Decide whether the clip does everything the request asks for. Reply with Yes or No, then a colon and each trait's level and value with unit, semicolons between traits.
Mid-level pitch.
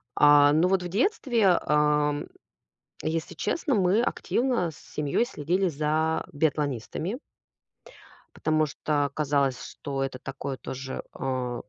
Yes: medium, 150 Hz